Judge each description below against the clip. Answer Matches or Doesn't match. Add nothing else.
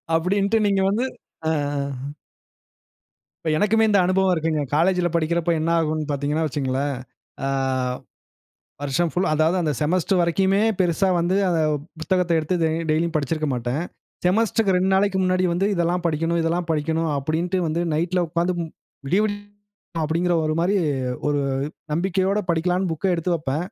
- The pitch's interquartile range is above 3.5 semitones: Doesn't match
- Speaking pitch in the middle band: Matches